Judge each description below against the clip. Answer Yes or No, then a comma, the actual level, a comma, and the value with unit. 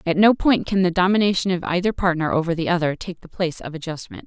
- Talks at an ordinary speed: No, fast, 240 wpm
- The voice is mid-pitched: Yes, medium, 175 Hz